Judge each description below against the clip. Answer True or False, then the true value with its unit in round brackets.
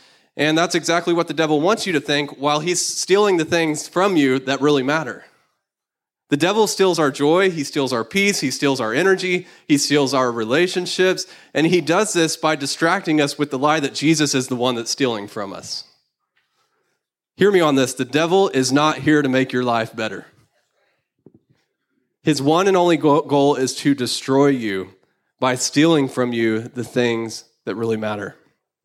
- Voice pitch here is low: False (145 Hz)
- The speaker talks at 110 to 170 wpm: False (185 wpm)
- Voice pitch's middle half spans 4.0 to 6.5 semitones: True (4.5 semitones)